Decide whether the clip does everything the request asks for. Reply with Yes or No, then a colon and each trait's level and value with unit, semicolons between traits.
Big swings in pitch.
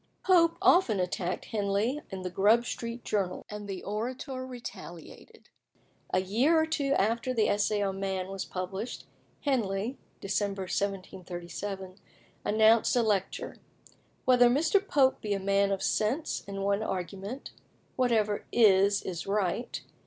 No: average, 4.0 semitones